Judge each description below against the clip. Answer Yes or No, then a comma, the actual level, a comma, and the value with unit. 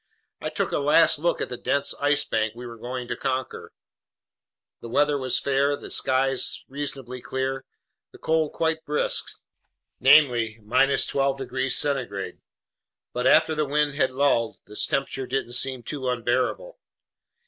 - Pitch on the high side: No, low, 135 Hz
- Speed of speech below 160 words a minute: Yes, average, 150 wpm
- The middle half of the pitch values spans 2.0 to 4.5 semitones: Yes, narrow, 2.5 semitones